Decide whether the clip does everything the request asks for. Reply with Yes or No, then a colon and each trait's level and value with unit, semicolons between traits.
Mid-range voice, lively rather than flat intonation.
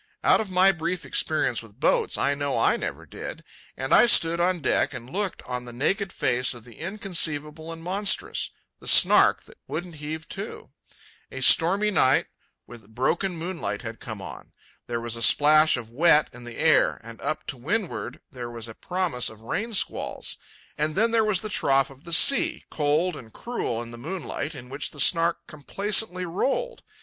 Yes: medium, 155 Hz; wide, 6.8 semitones